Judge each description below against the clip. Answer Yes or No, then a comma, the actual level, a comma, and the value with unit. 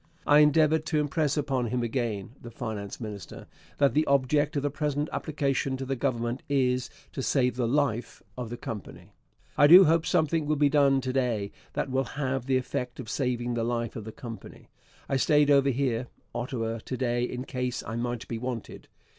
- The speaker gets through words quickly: No, average, 195 wpm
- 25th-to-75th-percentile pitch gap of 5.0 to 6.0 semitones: No, average, 3.3 semitones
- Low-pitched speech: Yes, low, 130 Hz